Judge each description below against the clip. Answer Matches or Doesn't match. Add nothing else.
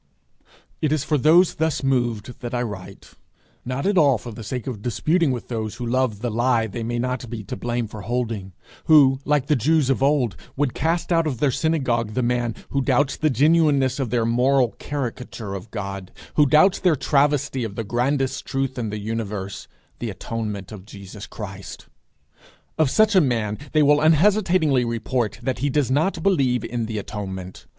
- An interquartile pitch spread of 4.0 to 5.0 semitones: Matches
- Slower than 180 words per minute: Doesn't match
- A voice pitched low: Matches